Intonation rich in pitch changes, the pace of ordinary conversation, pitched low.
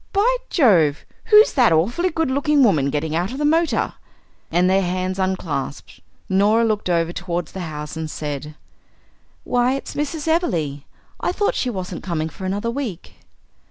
No: wide, 9.0 semitones; average, 160 wpm; high, 190 Hz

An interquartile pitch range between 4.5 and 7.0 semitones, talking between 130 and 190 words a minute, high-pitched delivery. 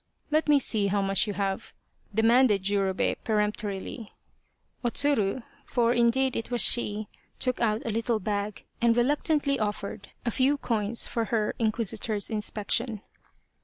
No: average, 2.8 semitones; average, 155 wpm; high, 225 Hz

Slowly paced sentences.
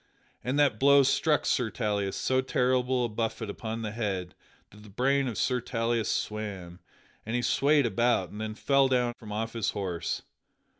No: average, 180 wpm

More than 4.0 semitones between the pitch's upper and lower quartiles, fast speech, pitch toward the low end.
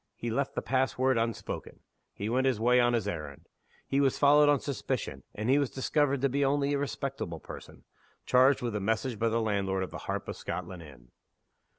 Yes: average, 4.8 semitones; fast, 210 wpm; low, 125 Hz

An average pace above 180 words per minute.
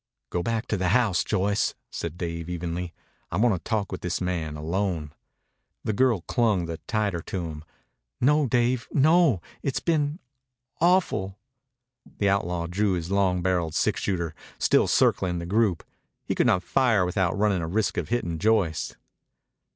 No: average, 160 wpm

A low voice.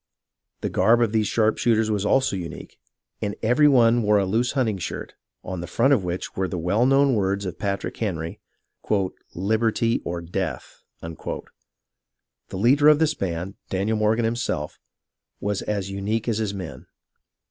Yes: low, 105 Hz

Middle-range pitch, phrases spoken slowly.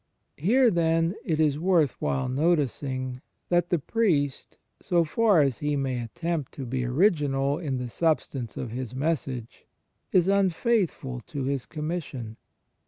No: medium, 150 Hz; average, 145 wpm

